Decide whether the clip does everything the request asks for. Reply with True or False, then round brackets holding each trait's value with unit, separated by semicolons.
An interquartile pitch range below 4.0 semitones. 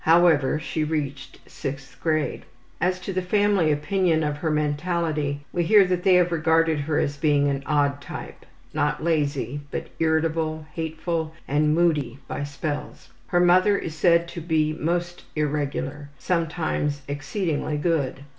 True (2.7 semitones)